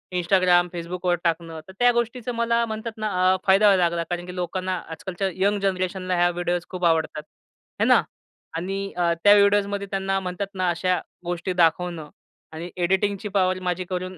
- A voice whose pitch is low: No, medium, 185 Hz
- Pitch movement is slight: Yes, narrow, 2.2 semitones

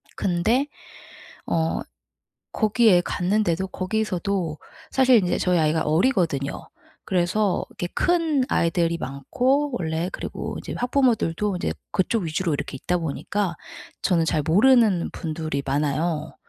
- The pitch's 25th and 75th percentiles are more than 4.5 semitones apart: Yes, average, 5.1 semitones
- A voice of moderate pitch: Yes, medium, 180 Hz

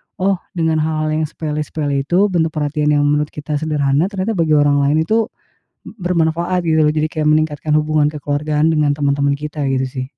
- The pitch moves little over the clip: Yes, narrow, 1.7 semitones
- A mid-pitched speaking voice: Yes, medium, 155 Hz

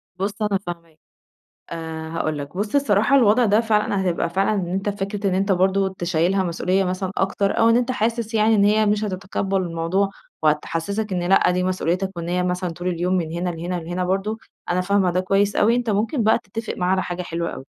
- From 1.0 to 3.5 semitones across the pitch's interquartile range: Yes, average, 2.8 semitones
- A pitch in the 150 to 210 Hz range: Yes, high, 190 Hz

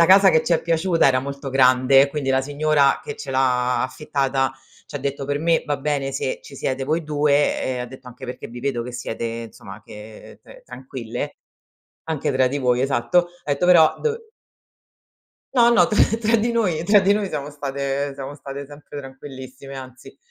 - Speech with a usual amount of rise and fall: Yes, average, 3.0 semitones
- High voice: No, medium, 140 Hz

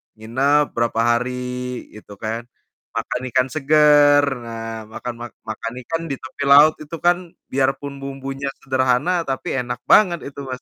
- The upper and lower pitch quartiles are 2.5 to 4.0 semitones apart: Yes, average, 2.9 semitones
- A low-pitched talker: Yes, low, 130 Hz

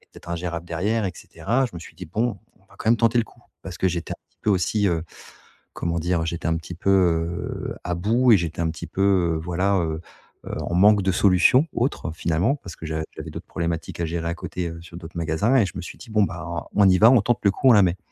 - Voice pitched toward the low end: Yes, very low, 90 Hz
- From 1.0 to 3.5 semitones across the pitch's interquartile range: No, average, 3.9 semitones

